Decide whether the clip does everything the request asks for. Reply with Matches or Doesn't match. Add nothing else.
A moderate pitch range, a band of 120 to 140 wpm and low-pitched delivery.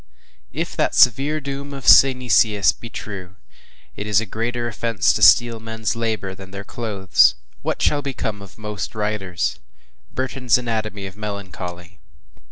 Doesn't match